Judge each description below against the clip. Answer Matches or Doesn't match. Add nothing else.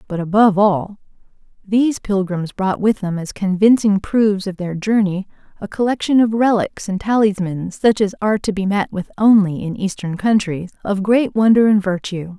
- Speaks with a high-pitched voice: Matches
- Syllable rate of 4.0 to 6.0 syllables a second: Doesn't match